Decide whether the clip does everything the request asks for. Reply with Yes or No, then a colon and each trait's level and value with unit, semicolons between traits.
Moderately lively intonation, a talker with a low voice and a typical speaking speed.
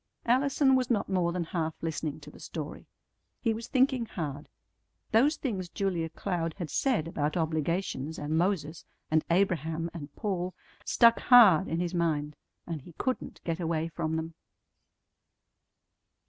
No: average, 4.3 semitones; medium, 170 Hz; average, 145 wpm